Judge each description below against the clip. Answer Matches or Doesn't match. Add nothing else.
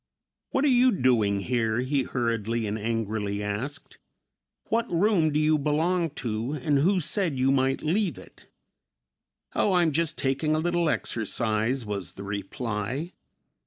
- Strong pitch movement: Matches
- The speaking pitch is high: Doesn't match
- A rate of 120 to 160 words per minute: Matches